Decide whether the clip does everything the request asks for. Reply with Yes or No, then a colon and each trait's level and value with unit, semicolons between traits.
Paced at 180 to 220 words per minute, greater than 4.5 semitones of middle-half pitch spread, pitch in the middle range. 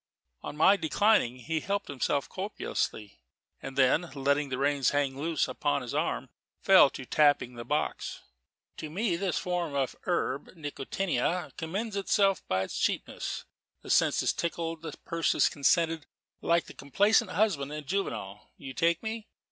No: average, 155 wpm; average, 4.9 semitones; medium, 160 Hz